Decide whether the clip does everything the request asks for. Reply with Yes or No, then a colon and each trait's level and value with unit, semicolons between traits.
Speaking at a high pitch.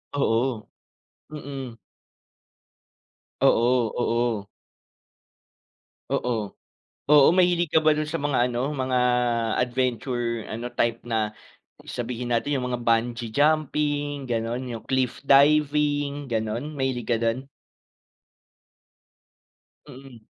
No: low, 125 Hz